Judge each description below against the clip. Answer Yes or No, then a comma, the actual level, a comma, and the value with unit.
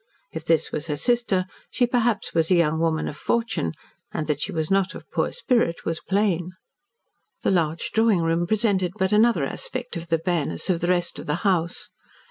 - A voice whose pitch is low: No, medium, 175 Hz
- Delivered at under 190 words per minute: No, average, 195 wpm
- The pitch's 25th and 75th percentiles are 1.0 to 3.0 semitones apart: No, average, 4.4 semitones